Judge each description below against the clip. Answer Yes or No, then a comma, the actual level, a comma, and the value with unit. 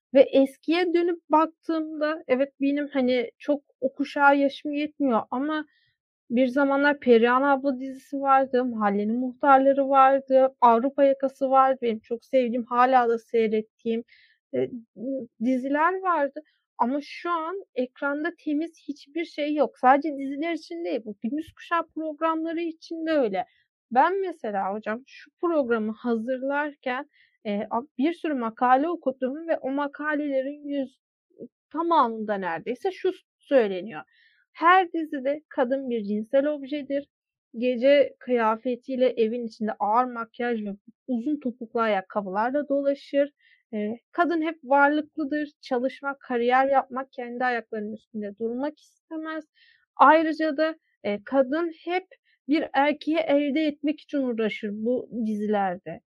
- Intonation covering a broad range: No, average, 4.1 semitones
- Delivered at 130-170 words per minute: No, average, 115 wpm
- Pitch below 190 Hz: No, very high, 275 Hz